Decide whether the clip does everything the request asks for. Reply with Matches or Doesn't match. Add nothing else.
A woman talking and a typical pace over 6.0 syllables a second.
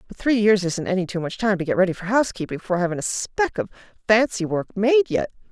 Matches